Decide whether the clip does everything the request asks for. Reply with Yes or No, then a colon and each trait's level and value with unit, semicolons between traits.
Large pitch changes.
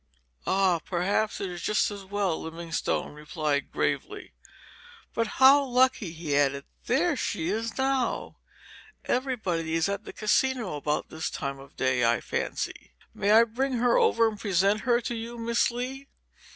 Yes: wide, 6.6 semitones